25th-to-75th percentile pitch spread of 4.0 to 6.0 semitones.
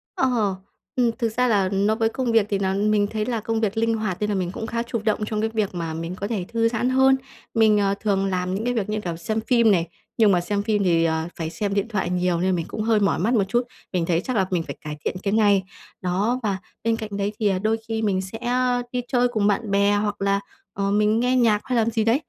No: average, 2.9 semitones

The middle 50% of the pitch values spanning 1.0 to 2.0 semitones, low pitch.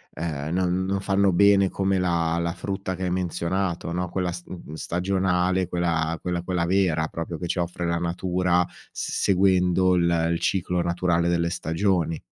Yes: narrow, 1.6 semitones; very low, 90 Hz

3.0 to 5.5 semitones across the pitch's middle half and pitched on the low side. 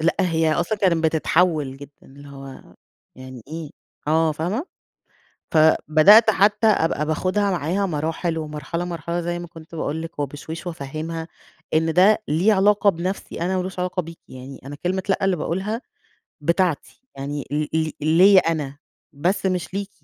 No: average, 3.4 semitones; medium, 165 Hz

